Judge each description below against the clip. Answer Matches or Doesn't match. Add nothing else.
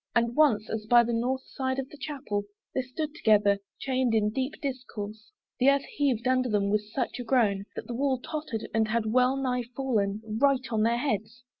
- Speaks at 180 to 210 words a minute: Matches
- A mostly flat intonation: Doesn't match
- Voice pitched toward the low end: Doesn't match